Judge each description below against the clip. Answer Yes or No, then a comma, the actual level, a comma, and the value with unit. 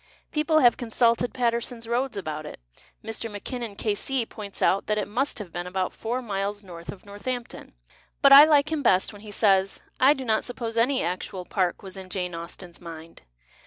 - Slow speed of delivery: No, average, 200 wpm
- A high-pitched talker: Yes, high, 215 Hz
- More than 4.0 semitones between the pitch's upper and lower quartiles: Yes, average, 4.5 semitones